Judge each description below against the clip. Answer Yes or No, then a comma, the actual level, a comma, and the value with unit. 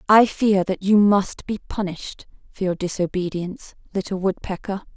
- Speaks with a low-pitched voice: No, high, 190 Hz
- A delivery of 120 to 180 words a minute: Yes, average, 145 wpm